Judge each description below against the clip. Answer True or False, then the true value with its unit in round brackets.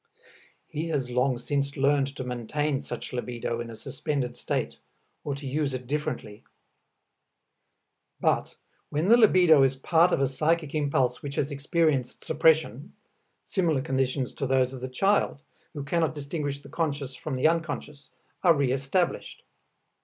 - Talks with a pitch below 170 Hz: True (140 Hz)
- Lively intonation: False (3.0 semitones)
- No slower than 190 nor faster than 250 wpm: False (145 wpm)